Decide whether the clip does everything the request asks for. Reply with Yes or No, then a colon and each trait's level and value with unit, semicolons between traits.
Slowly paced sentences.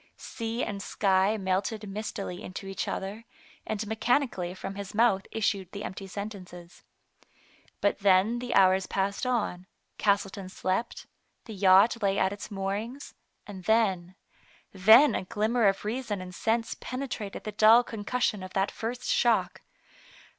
No: average, 145 wpm